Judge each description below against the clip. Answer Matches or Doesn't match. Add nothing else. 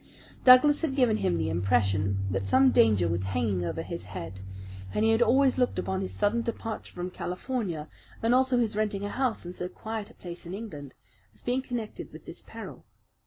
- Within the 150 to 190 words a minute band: Doesn't match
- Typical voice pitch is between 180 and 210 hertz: Matches